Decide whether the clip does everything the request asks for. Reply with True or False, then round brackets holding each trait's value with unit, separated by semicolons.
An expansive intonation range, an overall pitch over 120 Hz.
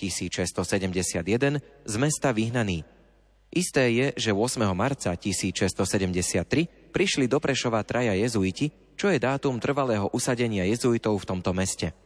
False (5.8 semitones; 110 Hz)